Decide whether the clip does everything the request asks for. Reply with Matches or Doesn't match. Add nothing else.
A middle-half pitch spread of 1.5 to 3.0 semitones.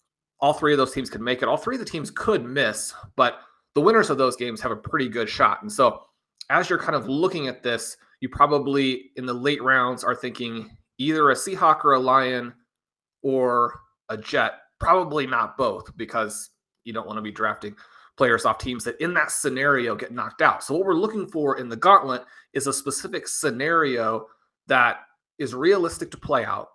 Matches